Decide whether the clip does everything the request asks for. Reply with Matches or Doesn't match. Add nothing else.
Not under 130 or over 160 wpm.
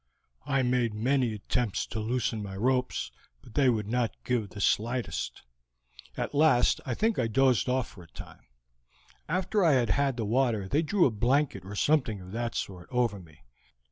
Doesn't match